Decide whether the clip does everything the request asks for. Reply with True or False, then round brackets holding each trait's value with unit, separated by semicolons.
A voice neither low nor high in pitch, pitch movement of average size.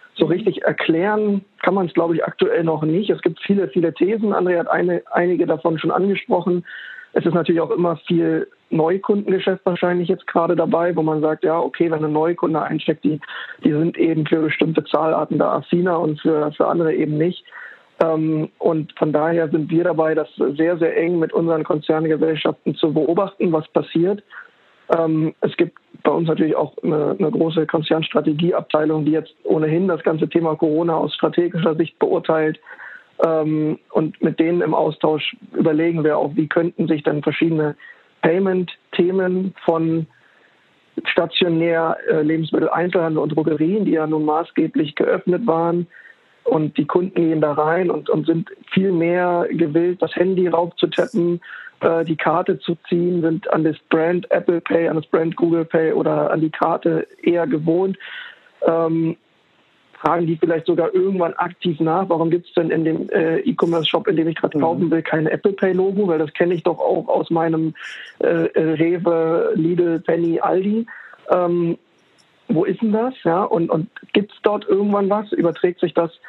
False (165 Hz; 1.9 semitones)